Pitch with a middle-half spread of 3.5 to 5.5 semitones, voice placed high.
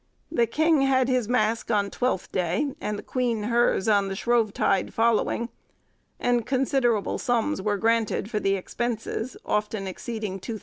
No: average, 2.8 semitones; high, 230 Hz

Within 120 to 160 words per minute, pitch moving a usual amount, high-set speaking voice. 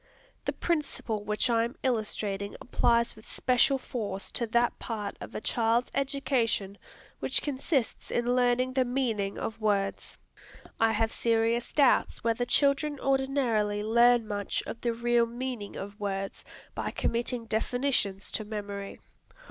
Yes: average, 140 wpm; average, 3.0 semitones; high, 230 Hz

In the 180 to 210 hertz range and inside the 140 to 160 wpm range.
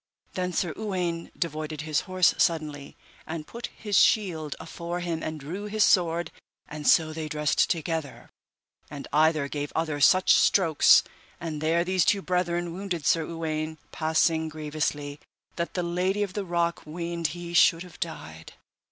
No: medium, 165 Hz; average, 155 wpm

